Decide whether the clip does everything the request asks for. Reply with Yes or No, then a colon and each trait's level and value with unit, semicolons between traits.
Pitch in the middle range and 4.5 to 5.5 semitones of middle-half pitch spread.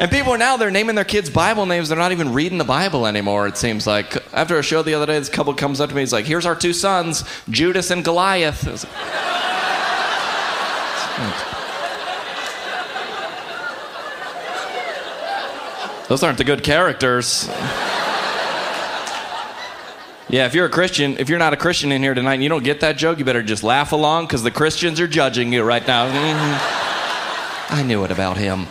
Yes: medium, 150 Hz; average, 4.9 semitones